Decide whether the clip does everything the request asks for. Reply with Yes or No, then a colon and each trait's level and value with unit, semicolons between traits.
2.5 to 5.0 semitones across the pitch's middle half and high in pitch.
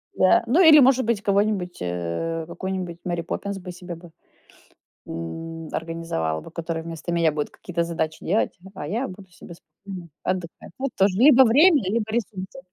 No: average, 3.8 semitones; medium, 180 Hz